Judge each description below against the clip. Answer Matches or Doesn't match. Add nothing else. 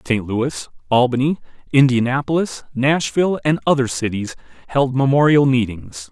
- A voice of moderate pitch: Doesn't match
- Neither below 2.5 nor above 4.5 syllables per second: Doesn't match